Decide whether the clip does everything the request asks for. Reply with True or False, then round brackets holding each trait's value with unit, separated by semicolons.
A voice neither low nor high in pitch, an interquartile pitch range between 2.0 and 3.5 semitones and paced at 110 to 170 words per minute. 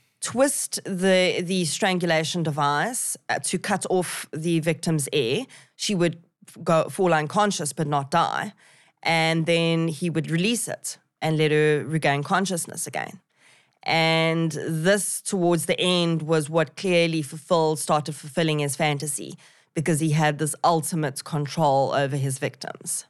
True (165 Hz; 2.4 semitones; 140 wpm)